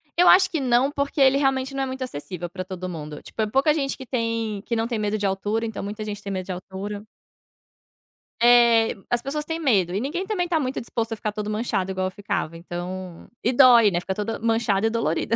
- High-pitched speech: Yes, high, 225 Hz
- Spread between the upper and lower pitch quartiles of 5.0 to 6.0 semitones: Yes, average, 5.3 semitones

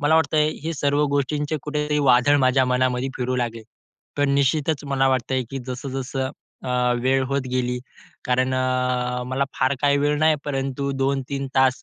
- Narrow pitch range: Yes, narrow, 1.9 semitones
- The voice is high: No, low, 135 Hz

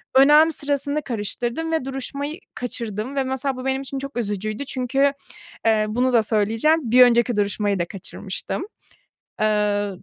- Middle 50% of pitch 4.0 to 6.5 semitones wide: Yes, average, 4.5 semitones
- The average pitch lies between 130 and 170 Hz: No, very high, 250 Hz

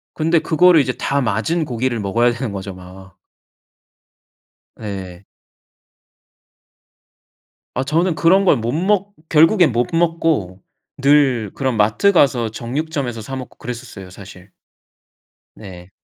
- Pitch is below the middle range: Yes, low, 125 Hz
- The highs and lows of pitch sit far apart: Yes, wide, 7.3 semitones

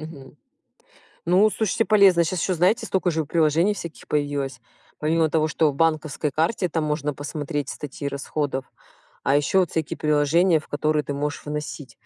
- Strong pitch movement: No, narrow, 2.6 semitones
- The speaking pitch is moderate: Yes, medium, 155 Hz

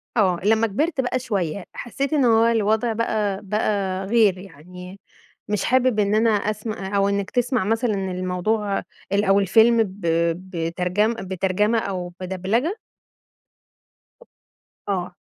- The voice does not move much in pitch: No, average, 3.2 semitones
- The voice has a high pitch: Yes, high, 205 Hz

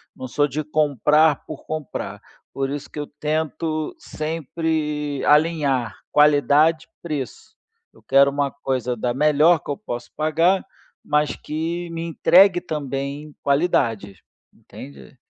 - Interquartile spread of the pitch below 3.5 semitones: Yes, narrow, 2.4 semitones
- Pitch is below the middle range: No, medium, 150 Hz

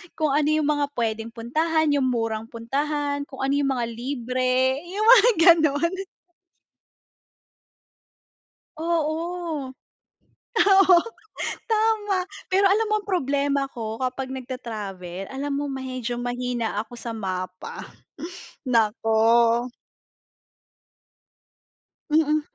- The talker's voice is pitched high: Yes, very high, 270 Hz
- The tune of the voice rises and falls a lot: No, average, 5.0 semitones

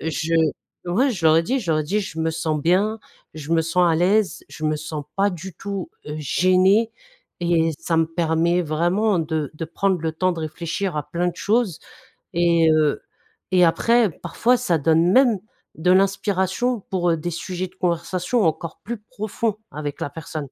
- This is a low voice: No, medium, 175 Hz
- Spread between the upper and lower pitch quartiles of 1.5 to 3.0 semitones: No, average, 3.4 semitones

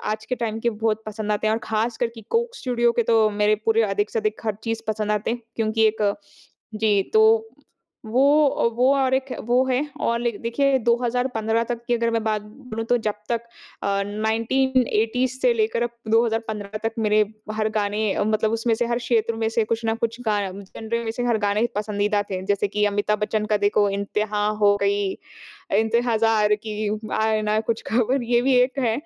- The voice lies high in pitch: Yes, high, 225 Hz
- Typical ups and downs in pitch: No, narrow, 2.0 semitones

